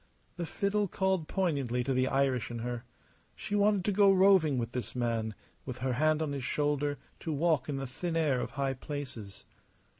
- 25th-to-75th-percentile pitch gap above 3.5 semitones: Yes, wide, 5.5 semitones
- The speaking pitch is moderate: Yes, medium, 145 Hz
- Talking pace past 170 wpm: Yes, average, 190 wpm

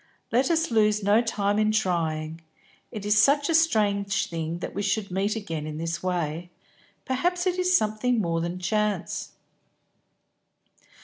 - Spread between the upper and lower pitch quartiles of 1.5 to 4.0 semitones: No, average, 4.9 semitones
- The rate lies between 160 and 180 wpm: No, average, 150 wpm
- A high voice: Yes, high, 205 Hz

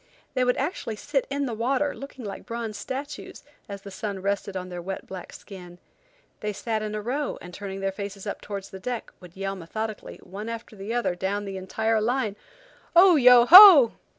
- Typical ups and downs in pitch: Yes, average, 4.2 semitones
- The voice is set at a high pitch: Yes, high, 215 Hz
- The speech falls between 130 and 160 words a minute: No, average, 200 wpm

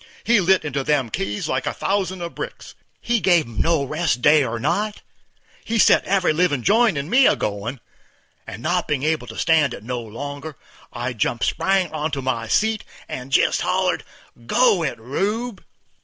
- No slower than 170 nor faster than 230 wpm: Yes, average, 185 wpm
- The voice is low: No, medium, 150 Hz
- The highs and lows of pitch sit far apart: Yes, wide, 7.1 semitones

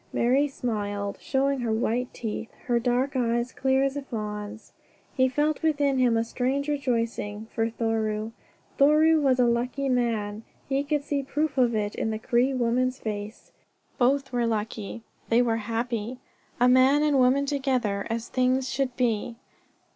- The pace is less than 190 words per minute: Yes, average, 160 wpm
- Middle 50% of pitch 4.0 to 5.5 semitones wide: No, average, 3.2 semitones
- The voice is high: Yes, high, 245 Hz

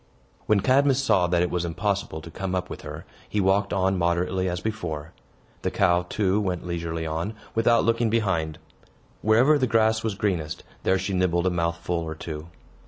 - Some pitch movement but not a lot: Yes, average, 3.8 semitones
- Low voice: Yes, very low, 95 Hz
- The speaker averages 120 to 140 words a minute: No, average, 180 wpm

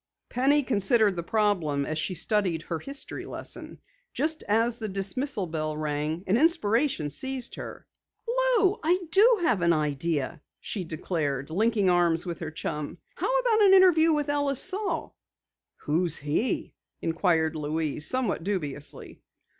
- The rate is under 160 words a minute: Yes, average, 145 wpm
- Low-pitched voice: No, high, 195 Hz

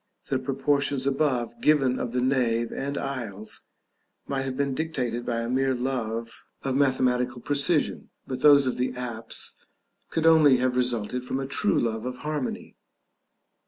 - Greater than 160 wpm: No, average, 155 wpm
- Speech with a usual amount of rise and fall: No, narrow, 2.3 semitones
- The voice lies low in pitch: Yes, low, 130 Hz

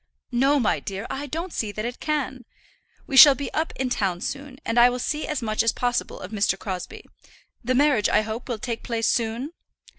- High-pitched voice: Yes, high, 245 Hz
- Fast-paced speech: Yes, fast, 210 wpm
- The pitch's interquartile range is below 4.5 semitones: Yes, average, 4.1 semitones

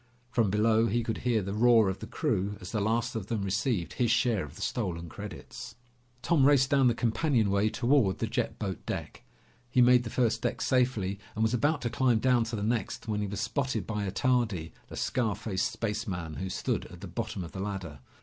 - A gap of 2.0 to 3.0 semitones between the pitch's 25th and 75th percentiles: No, average, 3.8 semitones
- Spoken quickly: Yes, fast, 215 wpm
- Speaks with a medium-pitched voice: No, low, 110 Hz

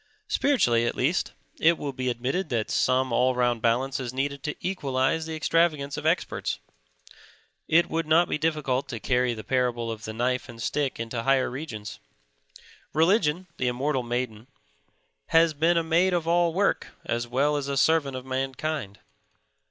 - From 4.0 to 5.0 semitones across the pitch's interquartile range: Yes, average, 4.5 semitones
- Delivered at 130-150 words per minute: No, average, 165 wpm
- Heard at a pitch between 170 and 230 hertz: No, low, 135 Hz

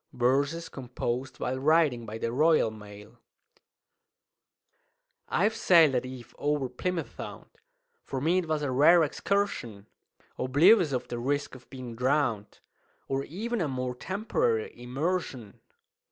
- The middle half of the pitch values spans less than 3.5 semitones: No, average, 5.1 semitones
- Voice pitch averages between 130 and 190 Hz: Yes, low, 135 Hz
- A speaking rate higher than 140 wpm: No, slow, 135 wpm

